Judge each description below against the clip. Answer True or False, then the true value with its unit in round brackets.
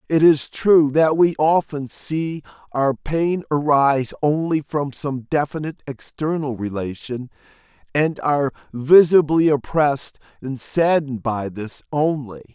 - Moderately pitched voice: True (145 Hz)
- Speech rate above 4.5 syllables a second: False (4.1 syllables/s)